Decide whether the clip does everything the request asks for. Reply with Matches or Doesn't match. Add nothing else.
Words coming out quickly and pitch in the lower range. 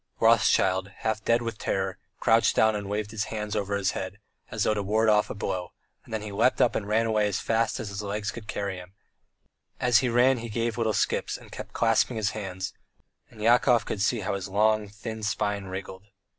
Matches